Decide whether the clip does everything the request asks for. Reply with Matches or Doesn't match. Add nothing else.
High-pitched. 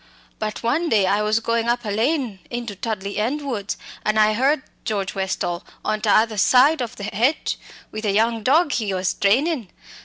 Matches